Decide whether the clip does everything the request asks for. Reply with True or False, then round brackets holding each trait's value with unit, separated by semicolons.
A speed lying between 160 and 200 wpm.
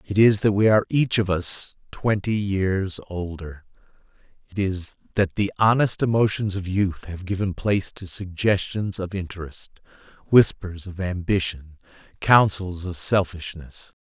False (135 wpm)